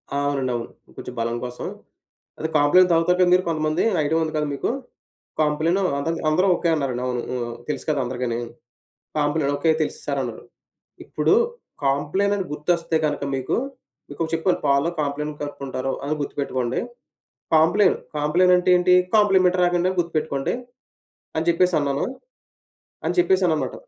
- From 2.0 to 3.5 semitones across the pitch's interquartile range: No, average, 4.1 semitones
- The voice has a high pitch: No, medium, 155 Hz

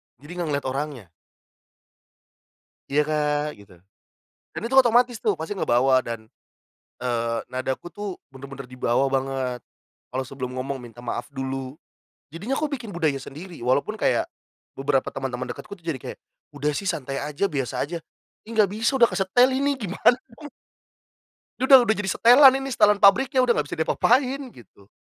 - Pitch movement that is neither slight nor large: No, wide, 8.2 semitones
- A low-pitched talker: No, medium, 150 Hz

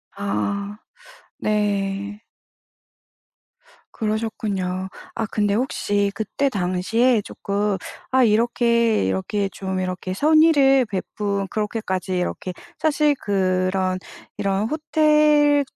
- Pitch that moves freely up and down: No, average, 4.1 semitones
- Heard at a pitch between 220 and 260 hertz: No, high, 205 Hz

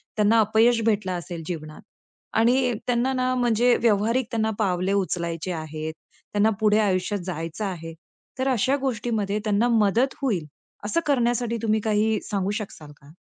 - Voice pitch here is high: Yes, high, 215 Hz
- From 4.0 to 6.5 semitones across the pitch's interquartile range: Yes, average, 4.3 semitones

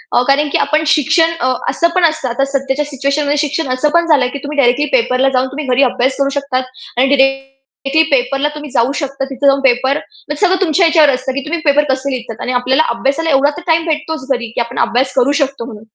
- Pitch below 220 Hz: No, very high, 275 Hz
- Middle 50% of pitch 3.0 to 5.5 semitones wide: No, narrow, 2.4 semitones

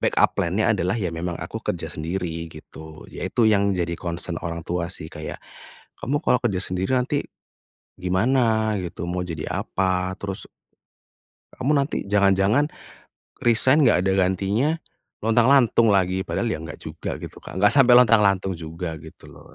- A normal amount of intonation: Yes, average, 4.9 semitones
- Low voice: Yes, very low, 95 Hz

